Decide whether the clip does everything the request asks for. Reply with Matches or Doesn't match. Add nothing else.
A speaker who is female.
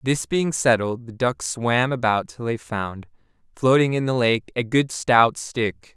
Doesn't match